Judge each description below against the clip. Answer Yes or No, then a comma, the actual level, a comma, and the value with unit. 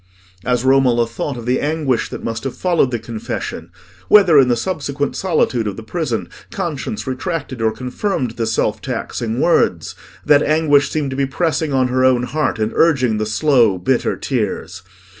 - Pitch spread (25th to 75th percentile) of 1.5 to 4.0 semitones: No, average, 4.4 semitones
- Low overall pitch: Yes, low, 130 Hz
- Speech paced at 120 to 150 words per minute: No, average, 165 wpm